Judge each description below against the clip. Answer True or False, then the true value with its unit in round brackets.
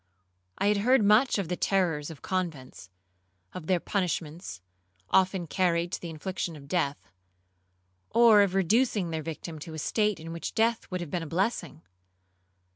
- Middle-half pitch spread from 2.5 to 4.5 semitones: True (4.0 semitones)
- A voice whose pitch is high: False (175 Hz)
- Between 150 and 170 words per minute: True (160 wpm)